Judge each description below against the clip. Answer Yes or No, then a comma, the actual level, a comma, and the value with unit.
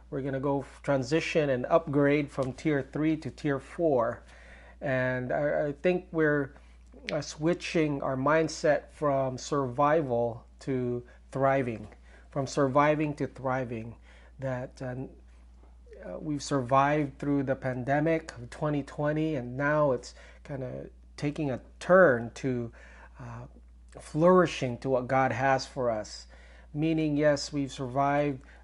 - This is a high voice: No, low, 135 Hz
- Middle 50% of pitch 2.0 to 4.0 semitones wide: Yes, average, 3.6 semitones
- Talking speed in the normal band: No, slow, 115 wpm